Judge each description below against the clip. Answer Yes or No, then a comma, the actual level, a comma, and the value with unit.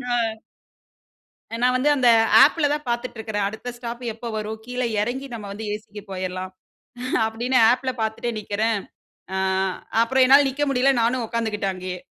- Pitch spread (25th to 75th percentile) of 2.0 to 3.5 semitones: Yes, average, 3.1 semitones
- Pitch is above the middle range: Yes, high, 230 Hz